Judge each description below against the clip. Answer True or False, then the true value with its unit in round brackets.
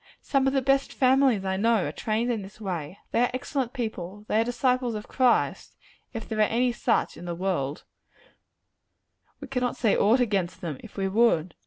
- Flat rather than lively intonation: False (4.5 semitones)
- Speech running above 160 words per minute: True (195 wpm)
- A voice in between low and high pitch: False (225 Hz)